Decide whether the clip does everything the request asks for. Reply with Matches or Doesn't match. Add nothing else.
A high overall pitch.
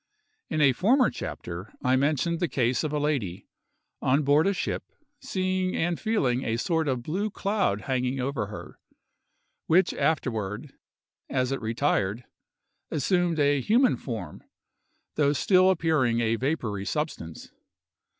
Doesn't match